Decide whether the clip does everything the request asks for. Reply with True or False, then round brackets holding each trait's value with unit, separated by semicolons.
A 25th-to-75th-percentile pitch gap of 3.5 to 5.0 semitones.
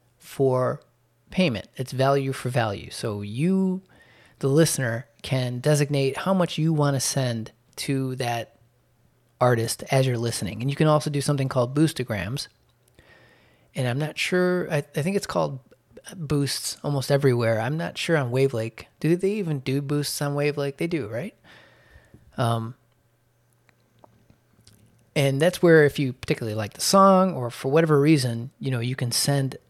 True (4.2 semitones)